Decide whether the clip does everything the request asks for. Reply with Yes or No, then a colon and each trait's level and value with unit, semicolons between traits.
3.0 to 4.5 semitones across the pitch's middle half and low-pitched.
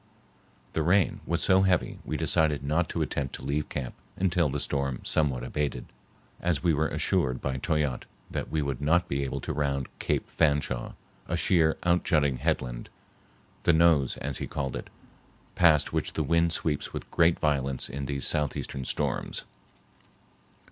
Yes: average, 3.4 semitones; very low, 75 Hz